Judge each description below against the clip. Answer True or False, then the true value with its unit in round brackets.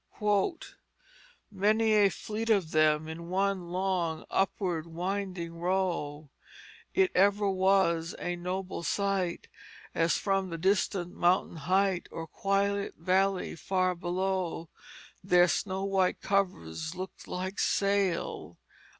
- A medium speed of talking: False (115 wpm)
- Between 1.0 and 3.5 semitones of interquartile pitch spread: True (2.5 semitones)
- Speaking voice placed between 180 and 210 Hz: True (185 Hz)